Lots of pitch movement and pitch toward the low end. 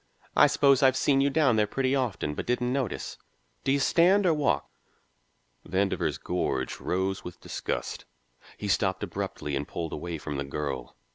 Yes: wide, 8.7 semitones; low, 105 Hz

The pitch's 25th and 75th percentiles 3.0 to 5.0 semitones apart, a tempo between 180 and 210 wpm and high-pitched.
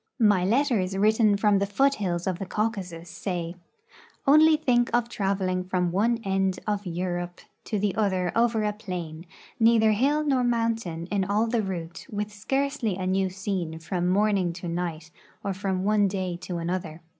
No: average, 3.6 semitones; average, 170 wpm; high, 195 Hz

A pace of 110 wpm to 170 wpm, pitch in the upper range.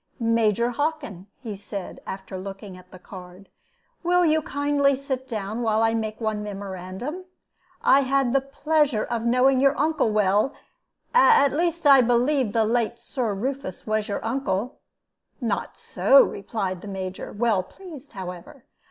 Yes: average, 150 wpm; high, 235 Hz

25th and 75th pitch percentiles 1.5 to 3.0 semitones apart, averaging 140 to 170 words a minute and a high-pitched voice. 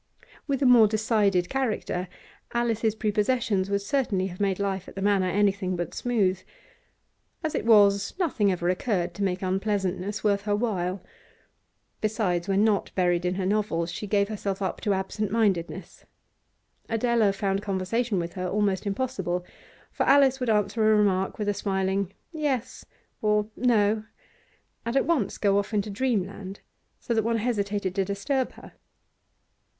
Yes: average, 2.7 semitones; average, 155 wpm; high, 205 Hz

